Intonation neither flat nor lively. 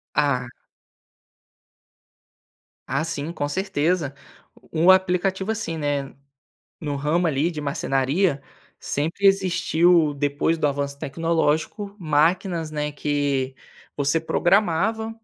Yes: average, 3.9 semitones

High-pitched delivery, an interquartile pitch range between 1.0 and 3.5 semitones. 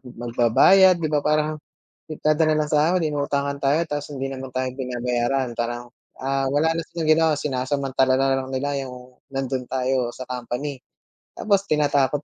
No: low, 135 Hz; average, 2.9 semitones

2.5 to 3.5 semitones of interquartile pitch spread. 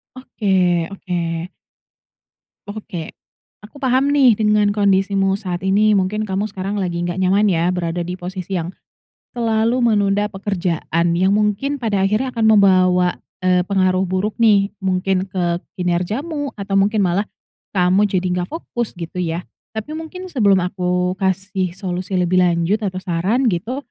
Yes: average, 2.8 semitones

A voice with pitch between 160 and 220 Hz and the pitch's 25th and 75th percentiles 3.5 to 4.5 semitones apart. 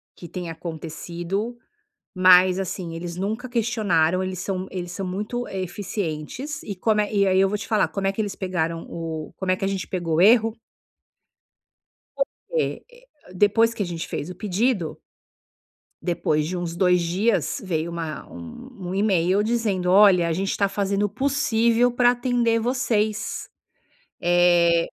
Yes: high, 190 Hz; average, 4.0 semitones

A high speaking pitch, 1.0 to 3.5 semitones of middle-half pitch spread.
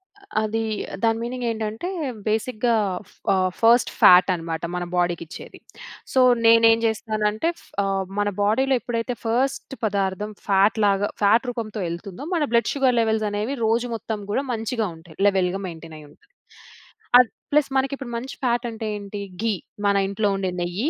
Yes: high, 220 Hz; average, 3.2 semitones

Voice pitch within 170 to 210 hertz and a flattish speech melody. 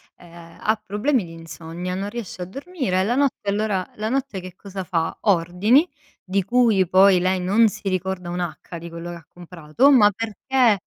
No: high, 190 Hz; average, 3.7 semitones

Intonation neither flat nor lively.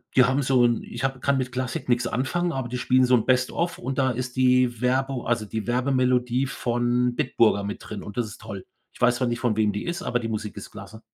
No: narrow, 1.7 semitones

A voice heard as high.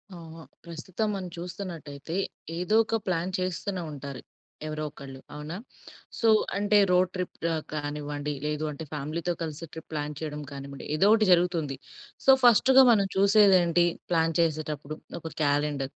No: medium, 165 Hz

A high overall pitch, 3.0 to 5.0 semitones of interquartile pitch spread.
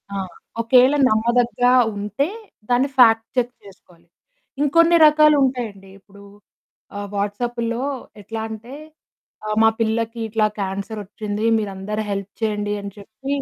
Yes: high, 220 Hz; average, 3.3 semitones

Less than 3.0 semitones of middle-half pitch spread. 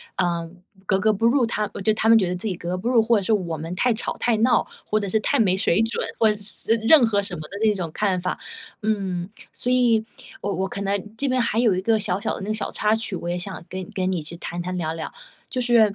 No: average, 3.5 semitones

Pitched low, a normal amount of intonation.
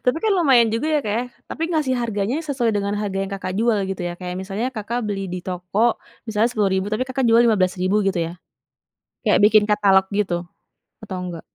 No: high, 210 Hz; average, 3.7 semitones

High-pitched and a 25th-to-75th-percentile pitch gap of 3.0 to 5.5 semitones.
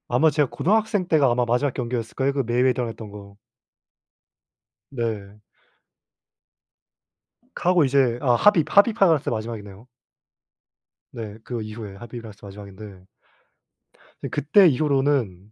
No: low, 120 Hz; average, 5.1 semitones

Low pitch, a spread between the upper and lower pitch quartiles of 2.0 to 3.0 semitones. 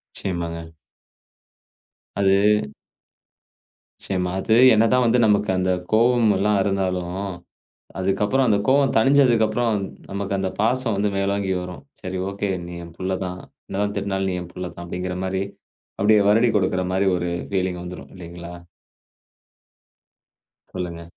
Yes: very low, 95 Hz; average, 2.7 semitones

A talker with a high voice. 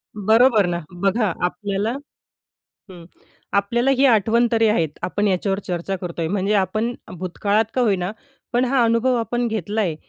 Yes: high, 210 Hz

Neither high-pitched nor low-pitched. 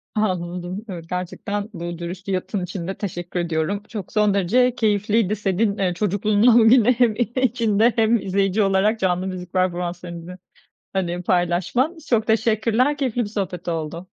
No: high, 195 Hz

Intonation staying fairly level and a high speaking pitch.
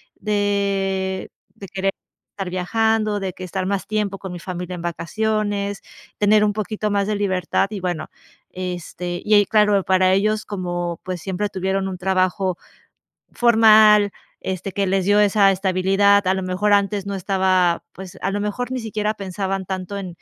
Yes: narrow, 1.9 semitones; high, 195 Hz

